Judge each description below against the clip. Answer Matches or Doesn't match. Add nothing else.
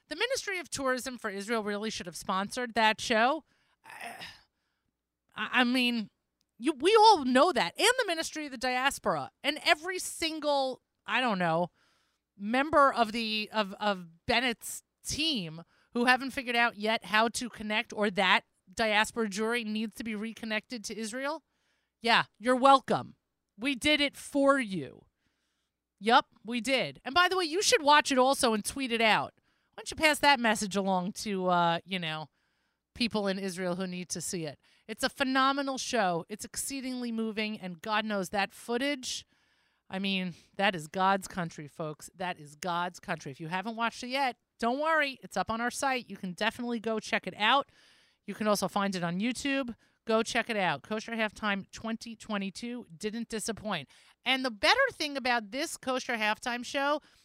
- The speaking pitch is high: Matches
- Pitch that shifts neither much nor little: Matches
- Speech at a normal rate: Matches